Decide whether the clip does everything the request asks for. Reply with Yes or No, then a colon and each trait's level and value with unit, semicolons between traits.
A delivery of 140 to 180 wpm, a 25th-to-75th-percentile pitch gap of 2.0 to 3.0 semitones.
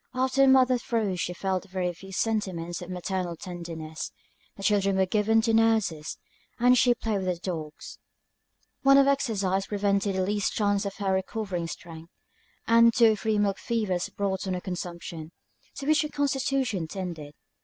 No: average, 170 wpm; average, 4.0 semitones